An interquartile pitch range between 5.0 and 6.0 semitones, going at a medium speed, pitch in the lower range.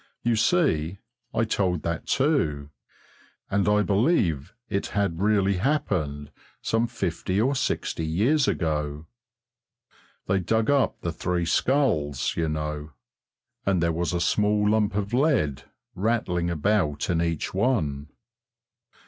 No: wide, 5.5 semitones; slow, 125 wpm; very low, 95 Hz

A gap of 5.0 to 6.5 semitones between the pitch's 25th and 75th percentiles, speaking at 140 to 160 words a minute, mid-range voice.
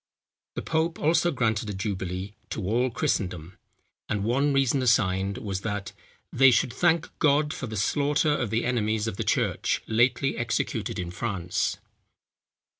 No: wide, 5.4 semitones; average, 150 wpm; low, 115 Hz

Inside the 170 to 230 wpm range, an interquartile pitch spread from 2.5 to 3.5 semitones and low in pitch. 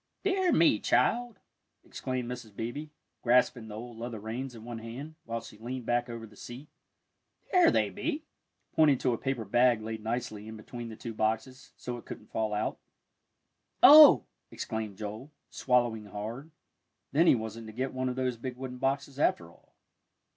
Yes: average, 175 wpm; average, 3.0 semitones; low, 120 Hz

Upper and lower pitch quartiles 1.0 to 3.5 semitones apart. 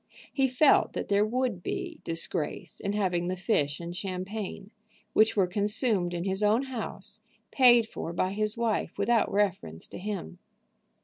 No: average, 4.2 semitones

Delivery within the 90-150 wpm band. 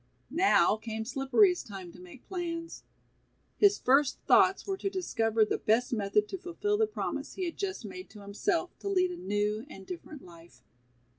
No: average, 175 wpm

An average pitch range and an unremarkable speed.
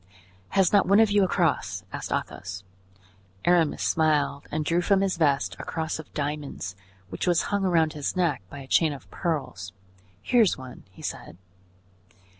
Yes: average, 4.5 semitones; average, 175 wpm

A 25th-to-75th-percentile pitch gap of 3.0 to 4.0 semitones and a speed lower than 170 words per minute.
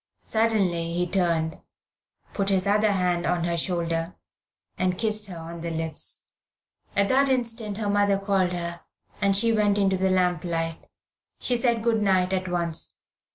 Yes: average, 3.4 semitones; average, 160 wpm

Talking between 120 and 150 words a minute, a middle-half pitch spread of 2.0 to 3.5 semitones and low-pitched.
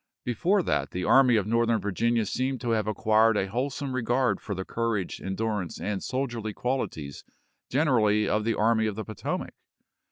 No: average, 165 wpm; average, 2.8 semitones; low, 115 Hz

